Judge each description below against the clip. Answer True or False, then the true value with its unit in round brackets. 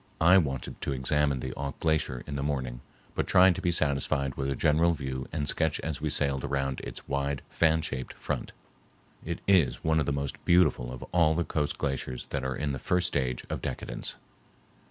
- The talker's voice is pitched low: True (70 Hz)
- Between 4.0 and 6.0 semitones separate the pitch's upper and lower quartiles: False (2.9 semitones)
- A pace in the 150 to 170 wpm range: False (200 wpm)